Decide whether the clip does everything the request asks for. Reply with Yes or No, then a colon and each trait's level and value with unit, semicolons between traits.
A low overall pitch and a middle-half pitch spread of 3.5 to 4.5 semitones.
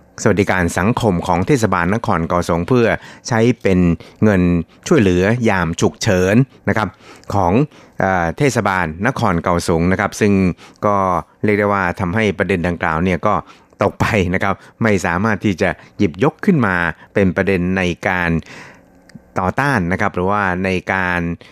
No: very low, 95 Hz; average, 3.0 semitones